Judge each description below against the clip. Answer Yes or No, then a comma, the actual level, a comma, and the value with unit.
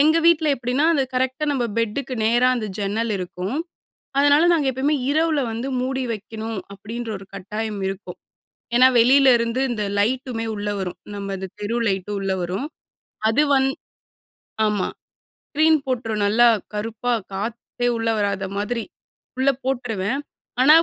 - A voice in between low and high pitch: No, high, 230 Hz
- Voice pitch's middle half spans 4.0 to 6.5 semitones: Yes, average, 4.3 semitones